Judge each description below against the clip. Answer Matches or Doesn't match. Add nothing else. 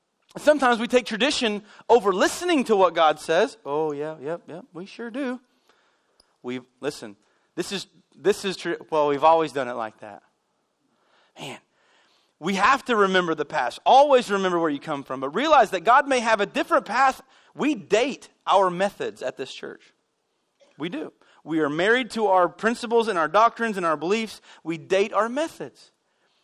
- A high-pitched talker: Matches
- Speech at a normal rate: Matches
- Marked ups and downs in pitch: Matches